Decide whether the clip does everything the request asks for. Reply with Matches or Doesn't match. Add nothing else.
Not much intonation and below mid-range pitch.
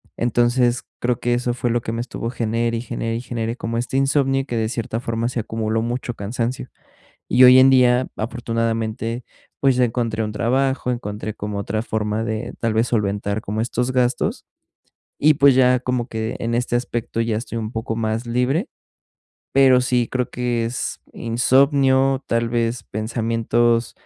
Matches